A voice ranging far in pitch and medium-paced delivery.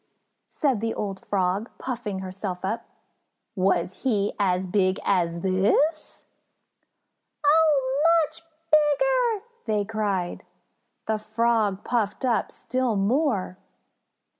No: wide, 5.9 semitones; slow, 100 wpm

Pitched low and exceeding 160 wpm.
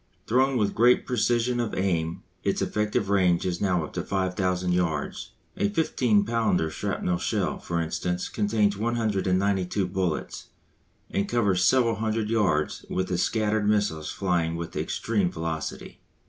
No: low, 100 Hz; average, 140 wpm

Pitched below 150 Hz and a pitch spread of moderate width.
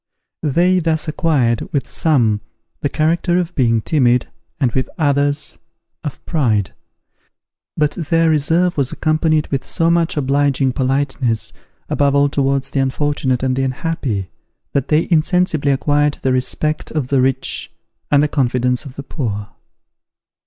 Yes: medium, 140 Hz; average, 3.3 semitones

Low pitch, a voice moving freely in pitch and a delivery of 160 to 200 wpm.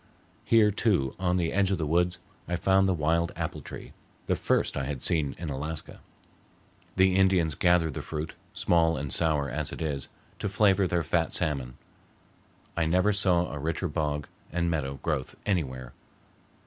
No: very low, 85 Hz; average, 3.8 semitones; average, 170 wpm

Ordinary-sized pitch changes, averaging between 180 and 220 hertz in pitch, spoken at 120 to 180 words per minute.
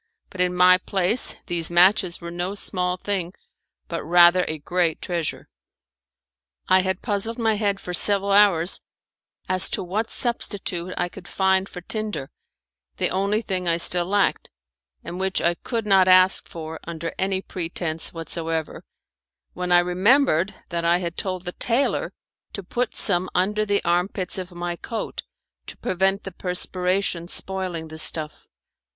No: narrow, 2.3 semitones; medium, 185 Hz; average, 155 wpm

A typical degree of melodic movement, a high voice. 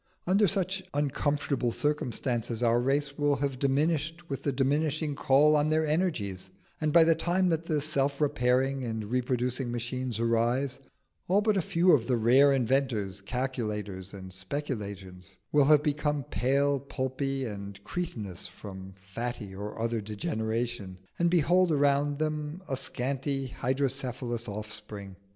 No: average, 4.6 semitones; low, 135 Hz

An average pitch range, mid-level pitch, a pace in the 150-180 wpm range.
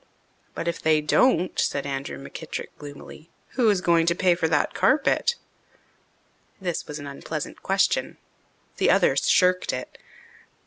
No: average, 4.5 semitones; medium, 170 Hz; average, 140 wpm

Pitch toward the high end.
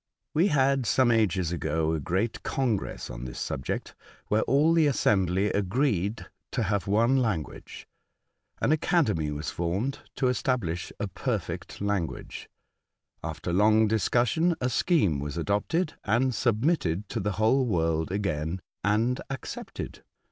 No: low, 105 Hz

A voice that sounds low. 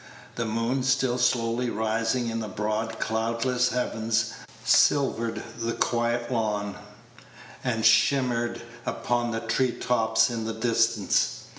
Yes: low, 115 Hz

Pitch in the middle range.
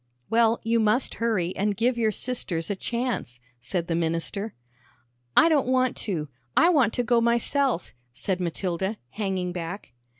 No: high, 210 Hz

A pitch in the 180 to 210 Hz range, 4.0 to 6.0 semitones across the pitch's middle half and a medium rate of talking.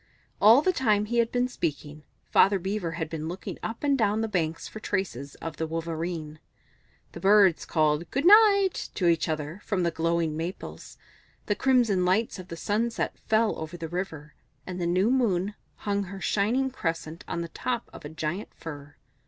Yes: medium, 185 Hz; average, 5.1 semitones; average, 185 wpm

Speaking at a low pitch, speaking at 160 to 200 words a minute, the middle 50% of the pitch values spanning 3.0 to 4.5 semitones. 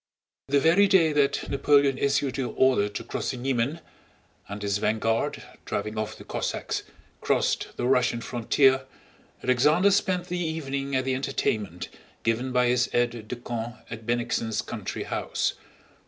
No: low, 130 Hz; average, 150 wpm; average, 3.3 semitones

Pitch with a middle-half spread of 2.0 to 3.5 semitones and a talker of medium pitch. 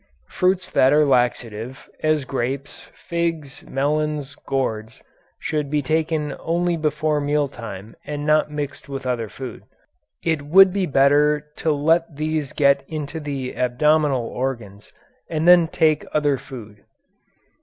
Yes: average, 2.7 semitones; medium, 145 Hz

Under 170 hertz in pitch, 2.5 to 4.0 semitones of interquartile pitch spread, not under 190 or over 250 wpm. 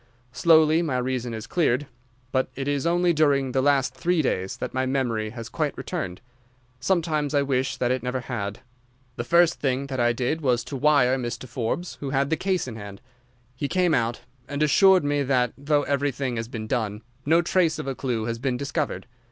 Yes: low, 135 Hz; average, 3.7 semitones; average, 200 wpm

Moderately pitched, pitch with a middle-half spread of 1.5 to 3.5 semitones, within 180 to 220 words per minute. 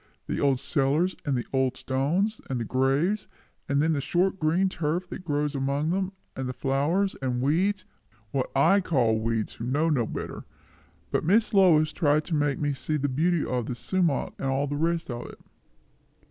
No: medium, 145 Hz; average, 4.4 semitones; average, 190 wpm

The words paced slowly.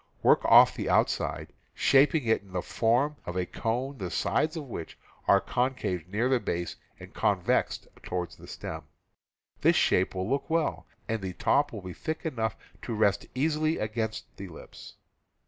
No: average, 170 wpm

